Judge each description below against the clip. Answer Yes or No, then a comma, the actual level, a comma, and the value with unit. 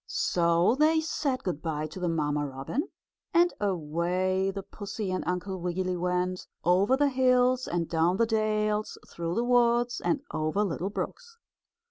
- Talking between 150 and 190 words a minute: Yes, average, 155 wpm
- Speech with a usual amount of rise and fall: No, wide, 5.9 semitones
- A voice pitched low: No, high, 190 Hz